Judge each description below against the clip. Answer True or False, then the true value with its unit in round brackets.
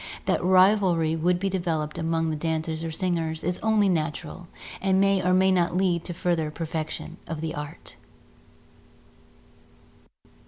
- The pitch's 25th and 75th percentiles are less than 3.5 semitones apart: True (2.5 semitones)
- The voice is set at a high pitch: False (170 Hz)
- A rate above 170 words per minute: False (145 wpm)